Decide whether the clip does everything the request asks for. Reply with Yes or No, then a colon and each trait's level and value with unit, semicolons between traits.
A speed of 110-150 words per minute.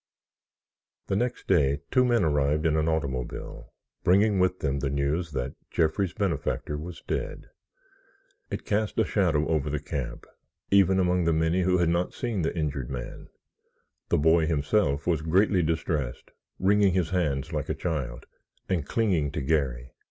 No: average, 160 wpm